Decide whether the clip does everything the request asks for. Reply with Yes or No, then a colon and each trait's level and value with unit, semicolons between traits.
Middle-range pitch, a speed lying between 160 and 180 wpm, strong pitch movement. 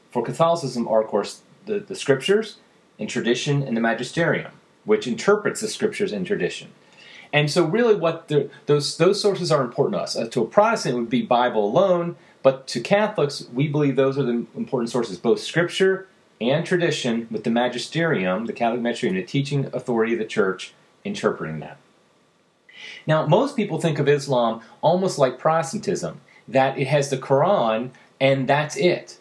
Yes: medium, 145 Hz; average, 175 wpm; wide, 7.2 semitones